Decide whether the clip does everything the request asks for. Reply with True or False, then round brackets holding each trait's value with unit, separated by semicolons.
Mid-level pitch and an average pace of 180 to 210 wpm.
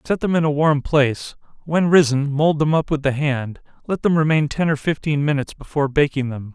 True (150 Hz; 200 wpm)